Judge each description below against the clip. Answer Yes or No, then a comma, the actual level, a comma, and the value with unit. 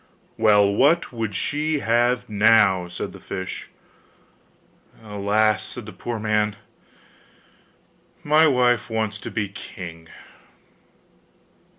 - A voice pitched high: No, low, 110 Hz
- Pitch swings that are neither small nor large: Yes, average, 3.1 semitones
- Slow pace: Yes, slow, 100 wpm